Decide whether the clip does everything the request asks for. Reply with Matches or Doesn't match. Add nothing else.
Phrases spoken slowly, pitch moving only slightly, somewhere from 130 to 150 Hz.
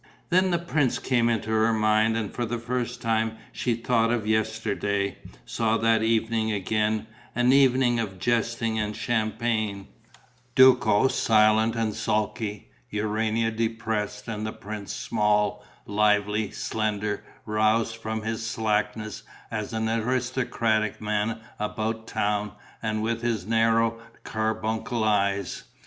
Doesn't match